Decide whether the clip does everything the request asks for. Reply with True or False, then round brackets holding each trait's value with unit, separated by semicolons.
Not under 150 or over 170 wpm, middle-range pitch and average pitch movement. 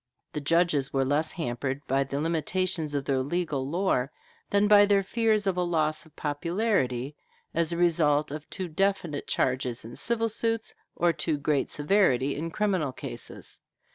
True (165 wpm; 160 Hz; 4.9 semitones)